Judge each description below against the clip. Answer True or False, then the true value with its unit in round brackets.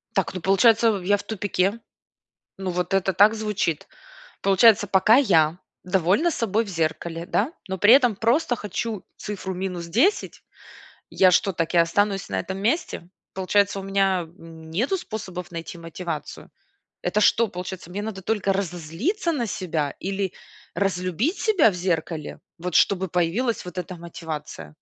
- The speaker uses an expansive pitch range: False (3.5 semitones)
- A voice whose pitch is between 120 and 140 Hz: False (190 Hz)